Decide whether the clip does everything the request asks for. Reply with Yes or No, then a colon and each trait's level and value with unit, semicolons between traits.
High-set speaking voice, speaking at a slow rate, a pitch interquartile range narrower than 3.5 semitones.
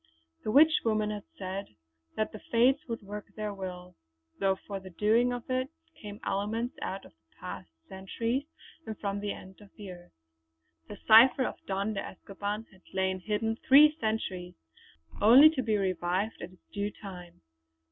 No: high, 210 Hz; average, 165 wpm; average, 3.1 semitones